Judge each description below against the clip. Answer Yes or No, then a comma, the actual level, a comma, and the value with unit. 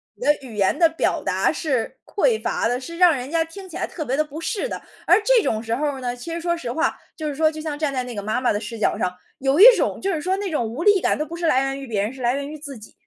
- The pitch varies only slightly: No, average, 5.2 semitones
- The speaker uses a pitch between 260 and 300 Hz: Yes, very high, 290 Hz